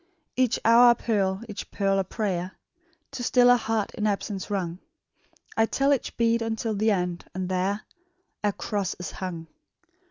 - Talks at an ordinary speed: Yes, average, 165 wpm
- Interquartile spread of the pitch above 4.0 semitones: No, average, 3.4 semitones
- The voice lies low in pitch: No, high, 210 Hz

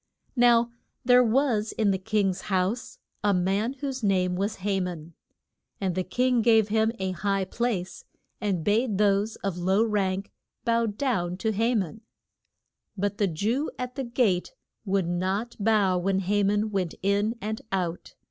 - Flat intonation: No, average, 3.2 semitones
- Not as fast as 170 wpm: Yes, average, 160 wpm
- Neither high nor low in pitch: No, high, 205 Hz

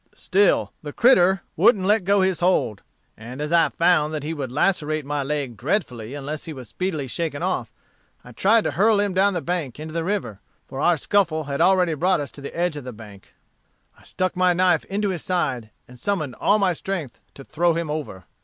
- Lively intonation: No, average, 4.9 semitones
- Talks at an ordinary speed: No, fast, 210 wpm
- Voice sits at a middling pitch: Yes, medium, 165 Hz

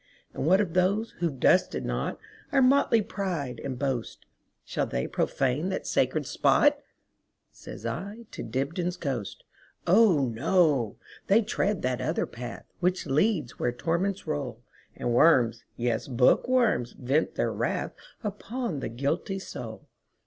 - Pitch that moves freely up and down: Yes, wide, 7.9 semitones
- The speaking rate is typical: No, slow, 120 wpm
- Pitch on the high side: No, medium, 165 Hz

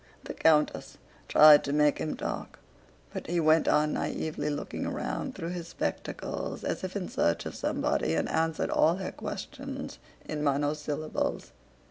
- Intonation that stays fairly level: Yes, narrow, 1.9 semitones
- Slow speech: No, average, 150 wpm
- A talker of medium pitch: Yes, medium, 155 Hz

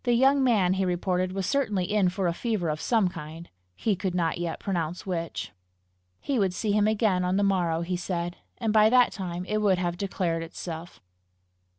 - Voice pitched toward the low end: No, medium, 185 Hz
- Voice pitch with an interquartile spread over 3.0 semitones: Yes, average, 3.4 semitones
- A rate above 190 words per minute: Yes, average, 200 wpm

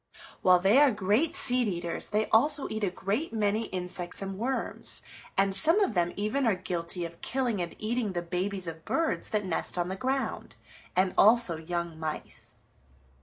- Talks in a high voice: Yes, high, 195 Hz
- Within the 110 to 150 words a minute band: No, average, 175 wpm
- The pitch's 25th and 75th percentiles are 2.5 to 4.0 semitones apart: No, average, 4.7 semitones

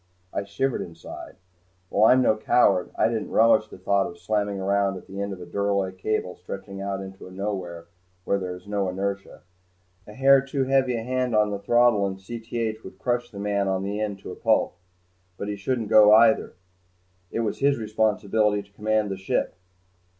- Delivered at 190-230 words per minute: Yes, average, 195 wpm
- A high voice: No, low, 100 Hz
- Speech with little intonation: Yes, narrow, 2.3 semitones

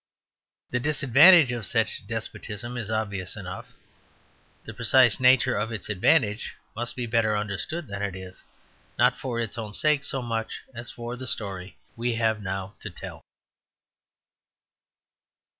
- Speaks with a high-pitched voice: No, low, 115 Hz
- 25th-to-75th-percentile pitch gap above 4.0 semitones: No, average, 3.2 semitones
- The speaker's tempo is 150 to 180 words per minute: No, average, 140 wpm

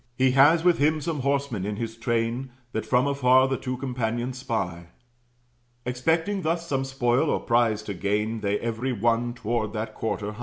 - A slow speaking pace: No, average, 180 wpm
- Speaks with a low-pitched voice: Yes, low, 125 Hz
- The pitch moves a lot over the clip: No, average, 3.3 semitones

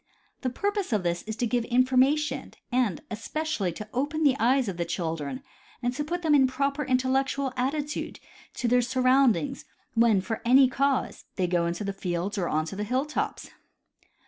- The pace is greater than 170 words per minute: Yes, average, 180 wpm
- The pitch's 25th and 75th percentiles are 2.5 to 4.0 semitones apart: No, average, 5.1 semitones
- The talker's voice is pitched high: Yes, very high, 255 Hz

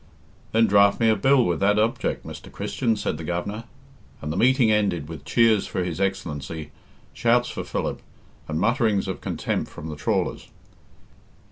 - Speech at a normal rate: Yes, average, 165 wpm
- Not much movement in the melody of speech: No, wide, 5.4 semitones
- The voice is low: Yes, low, 100 Hz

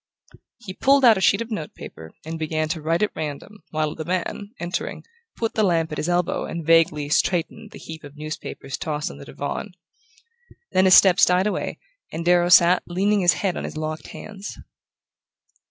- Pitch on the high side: No, medium, 175 Hz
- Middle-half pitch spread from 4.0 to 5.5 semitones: No, average, 3.6 semitones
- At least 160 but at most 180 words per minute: No, average, 190 wpm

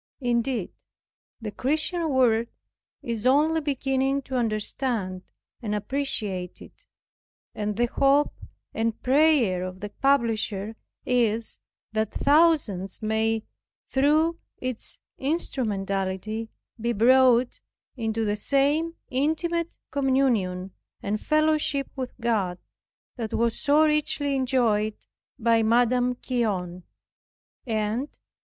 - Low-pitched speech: No, high, 240 Hz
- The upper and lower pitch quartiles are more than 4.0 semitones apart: Yes, average, 4.4 semitones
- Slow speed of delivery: Yes, slow, 100 wpm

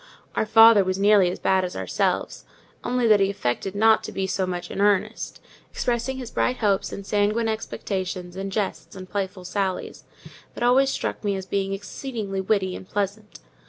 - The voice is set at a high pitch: Yes, high, 200 Hz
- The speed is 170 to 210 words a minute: Yes, average, 180 wpm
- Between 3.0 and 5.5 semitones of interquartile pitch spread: No, narrow, 2.5 semitones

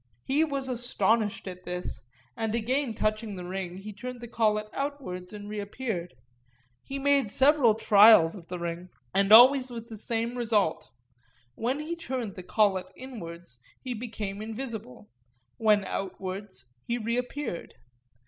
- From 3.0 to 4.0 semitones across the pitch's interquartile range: No, average, 4.8 semitones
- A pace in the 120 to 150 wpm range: Yes, average, 140 wpm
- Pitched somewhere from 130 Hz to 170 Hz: No, high, 215 Hz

